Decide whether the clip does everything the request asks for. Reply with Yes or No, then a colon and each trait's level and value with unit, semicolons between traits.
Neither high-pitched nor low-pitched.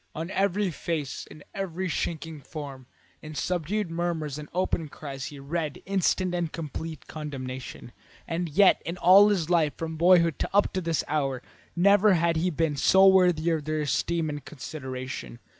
Yes: medium, 165 Hz